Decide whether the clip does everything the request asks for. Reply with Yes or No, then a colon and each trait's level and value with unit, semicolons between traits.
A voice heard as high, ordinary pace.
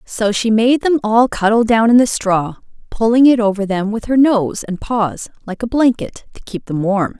No: high, 220 Hz; fast, 215 wpm